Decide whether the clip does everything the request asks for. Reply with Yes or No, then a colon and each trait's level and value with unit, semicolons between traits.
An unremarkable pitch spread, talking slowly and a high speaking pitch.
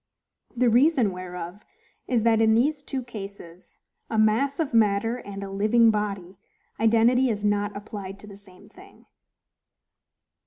Yes: average, 3.1 semitones; slow, 130 wpm; high, 215 Hz